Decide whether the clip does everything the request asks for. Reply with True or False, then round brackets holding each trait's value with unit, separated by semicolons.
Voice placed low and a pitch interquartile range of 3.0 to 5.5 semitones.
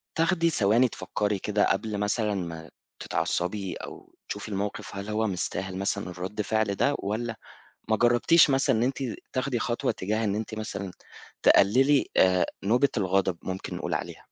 True (105 Hz; 3.5 semitones)